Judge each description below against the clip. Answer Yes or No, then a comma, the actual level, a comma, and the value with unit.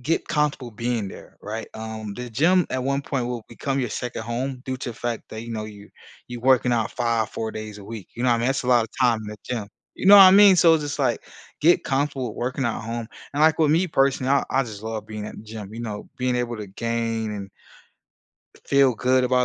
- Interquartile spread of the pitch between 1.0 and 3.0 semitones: No, average, 3.4 semitones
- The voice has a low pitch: Yes, low, 120 Hz